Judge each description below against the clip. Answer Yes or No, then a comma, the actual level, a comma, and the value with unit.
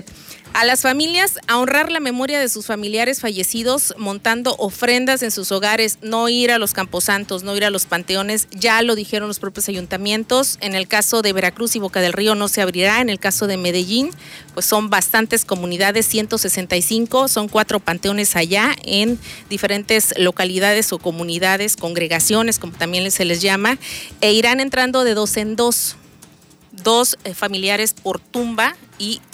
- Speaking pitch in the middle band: No, high, 210 Hz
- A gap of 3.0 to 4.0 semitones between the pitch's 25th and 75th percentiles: Yes, average, 3.3 semitones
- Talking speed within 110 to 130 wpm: No, average, 165 wpm